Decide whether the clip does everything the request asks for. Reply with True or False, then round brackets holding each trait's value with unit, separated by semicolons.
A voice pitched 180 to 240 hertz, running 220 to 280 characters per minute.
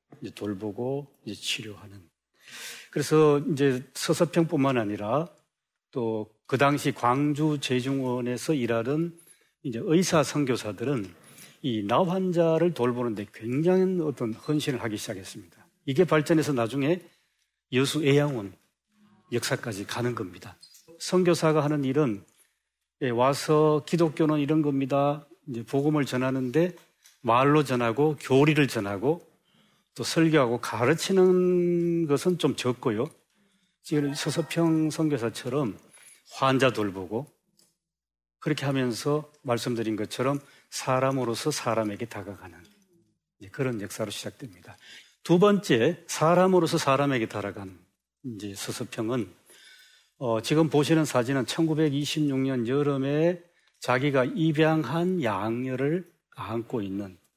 False (140 Hz; 250 characters per minute)